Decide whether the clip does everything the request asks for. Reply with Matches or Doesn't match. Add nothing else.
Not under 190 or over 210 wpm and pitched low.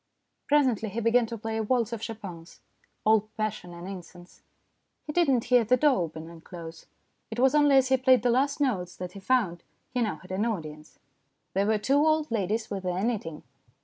Doesn't match